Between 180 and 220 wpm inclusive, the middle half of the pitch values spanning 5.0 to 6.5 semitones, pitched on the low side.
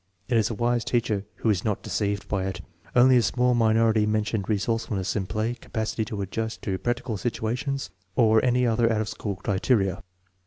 No: average, 185 wpm; average, 2.7 semitones; low, 110 Hz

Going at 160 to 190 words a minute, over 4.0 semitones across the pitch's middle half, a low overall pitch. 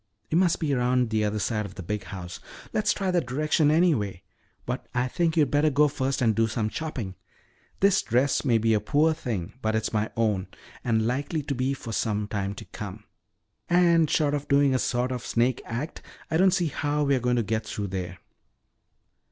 No: fast, 205 wpm; wide, 5.6 semitones; low, 125 Hz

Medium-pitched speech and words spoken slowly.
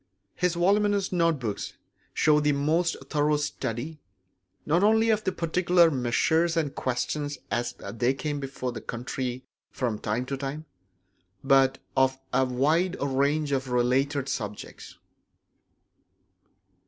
Yes: medium, 145 Hz; slow, 120 wpm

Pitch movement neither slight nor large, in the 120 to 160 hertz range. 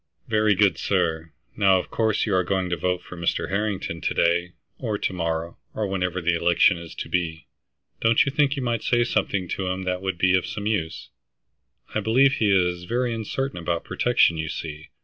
No: average, 3.9 semitones; very low, 95 Hz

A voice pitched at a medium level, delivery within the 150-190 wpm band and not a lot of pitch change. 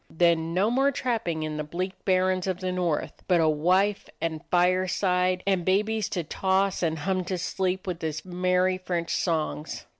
Yes: medium, 180 Hz; average, 180 wpm; narrow, 2.0 semitones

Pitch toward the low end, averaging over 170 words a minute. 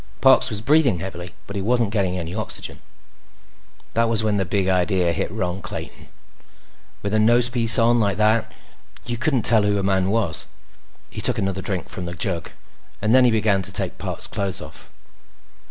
Yes: low, 100 Hz; average, 180 wpm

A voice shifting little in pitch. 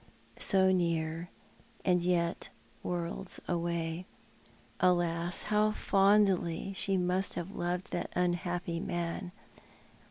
Yes: narrow, 1.8 semitones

